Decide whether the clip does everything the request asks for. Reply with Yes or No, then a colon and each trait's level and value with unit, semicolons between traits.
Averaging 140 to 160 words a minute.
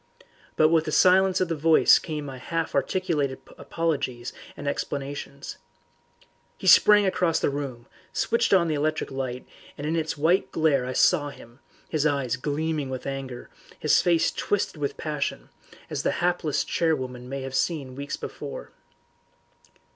Yes: average, 155 wpm